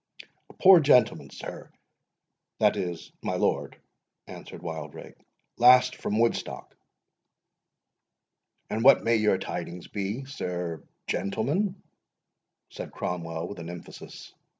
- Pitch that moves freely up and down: Yes, wide, 6.4 semitones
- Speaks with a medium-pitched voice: No, low, 110 Hz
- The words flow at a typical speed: No, slow, 100 wpm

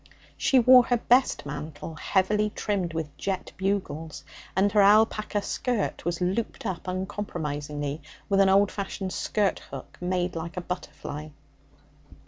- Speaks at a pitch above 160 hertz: Yes, high, 190 Hz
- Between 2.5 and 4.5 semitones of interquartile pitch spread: Yes, average, 4.1 semitones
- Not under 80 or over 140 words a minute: Yes, slow, 135 wpm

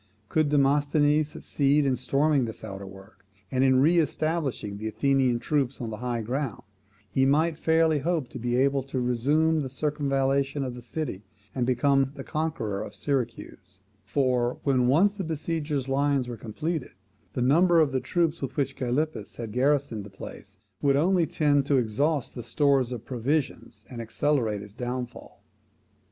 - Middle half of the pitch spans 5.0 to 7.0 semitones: No, average, 3.5 semitones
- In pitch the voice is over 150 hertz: No, low, 135 Hz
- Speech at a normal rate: Yes, average, 165 wpm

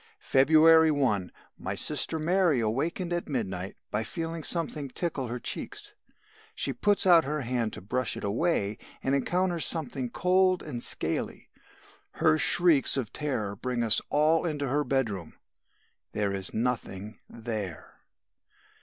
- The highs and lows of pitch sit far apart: Yes, wide, 6.7 semitones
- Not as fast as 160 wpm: Yes, slow, 135 wpm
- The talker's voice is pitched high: No, low, 135 Hz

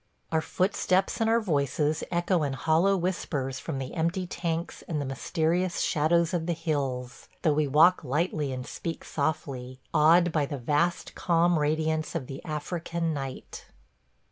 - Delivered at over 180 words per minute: No, average, 155 wpm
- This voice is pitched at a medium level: Yes, medium, 160 Hz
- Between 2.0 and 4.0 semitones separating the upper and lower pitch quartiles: Yes, average, 3.2 semitones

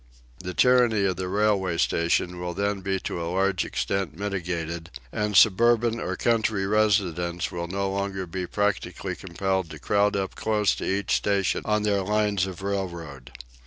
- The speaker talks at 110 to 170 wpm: Yes, average, 160 wpm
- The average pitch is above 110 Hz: No, very low, 95 Hz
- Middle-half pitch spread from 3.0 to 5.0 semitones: No, narrow, 2.6 semitones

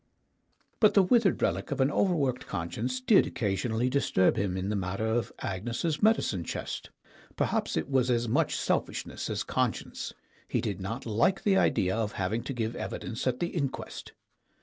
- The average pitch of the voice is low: Yes, low, 120 Hz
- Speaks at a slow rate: No, average, 170 wpm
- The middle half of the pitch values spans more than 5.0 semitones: Yes, wide, 5.4 semitones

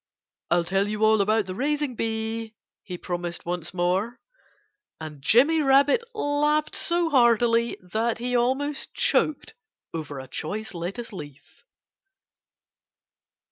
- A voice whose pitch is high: Yes, high, 220 Hz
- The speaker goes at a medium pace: No, slow, 120 wpm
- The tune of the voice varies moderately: No, wide, 6.8 semitones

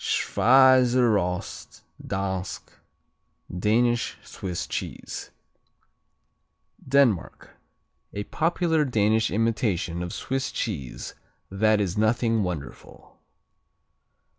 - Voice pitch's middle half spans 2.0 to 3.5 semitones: No, average, 4.4 semitones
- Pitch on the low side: Yes, low, 110 Hz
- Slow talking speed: Yes, slow, 75 wpm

